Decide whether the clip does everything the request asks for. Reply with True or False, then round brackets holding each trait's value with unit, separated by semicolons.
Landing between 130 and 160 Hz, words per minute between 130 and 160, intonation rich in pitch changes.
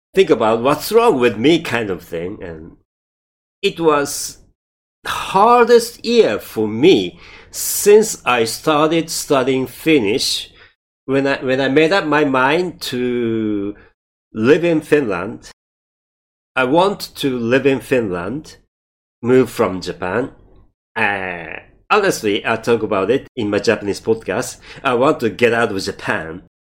True (135 Hz; 135 wpm; 5.9 semitones)